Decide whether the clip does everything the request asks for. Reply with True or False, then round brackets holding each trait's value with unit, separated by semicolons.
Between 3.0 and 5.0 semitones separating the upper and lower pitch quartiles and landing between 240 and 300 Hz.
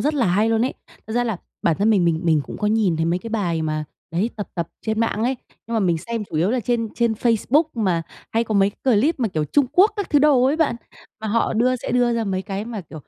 False (4.5 semitones; 220 Hz)